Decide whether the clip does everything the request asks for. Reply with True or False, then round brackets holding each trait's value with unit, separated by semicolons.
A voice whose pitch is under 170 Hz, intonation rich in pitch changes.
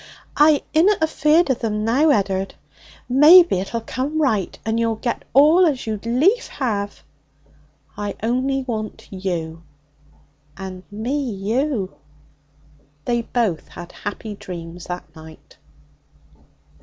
False (230 Hz; 6.1 semitones)